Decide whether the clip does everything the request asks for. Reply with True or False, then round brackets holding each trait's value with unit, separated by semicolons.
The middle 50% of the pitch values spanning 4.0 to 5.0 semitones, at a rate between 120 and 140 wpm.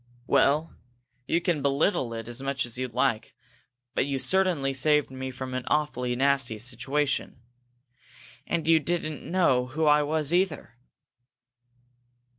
False (3.4 semitones; 135 wpm)